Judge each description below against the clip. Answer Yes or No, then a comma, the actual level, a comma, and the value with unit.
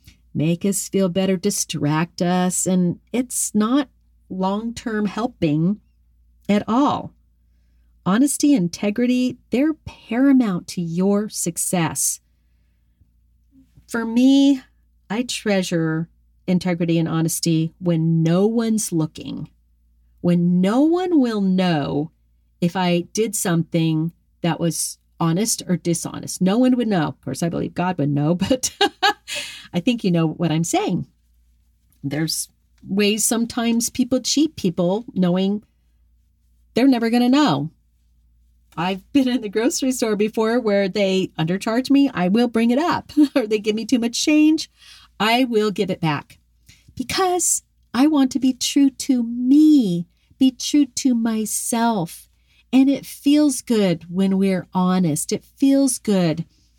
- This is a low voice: No, high, 190 Hz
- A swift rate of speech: No, slow, 135 wpm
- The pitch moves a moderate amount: No, wide, 7.2 semitones